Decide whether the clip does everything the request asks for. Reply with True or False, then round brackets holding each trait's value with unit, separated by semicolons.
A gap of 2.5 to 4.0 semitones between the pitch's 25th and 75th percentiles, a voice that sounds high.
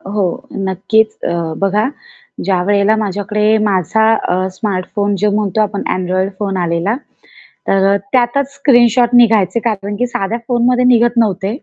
True (3.3 semitones; 210 Hz)